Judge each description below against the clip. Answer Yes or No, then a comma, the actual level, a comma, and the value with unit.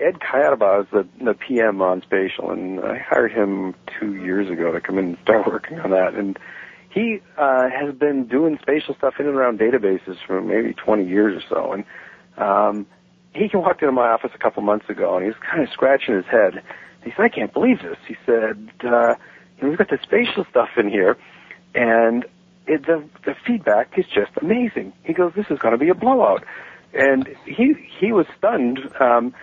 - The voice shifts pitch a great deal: Yes, wide, 8.0 semitones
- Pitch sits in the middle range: No, low, 125 Hz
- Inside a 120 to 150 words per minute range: No, average, 200 wpm